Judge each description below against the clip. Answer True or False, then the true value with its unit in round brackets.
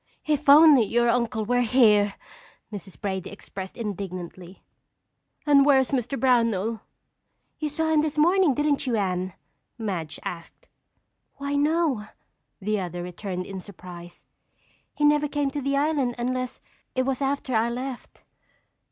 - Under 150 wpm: True (140 wpm)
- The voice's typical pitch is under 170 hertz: False (245 Hz)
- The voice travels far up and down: True (6.2 semitones)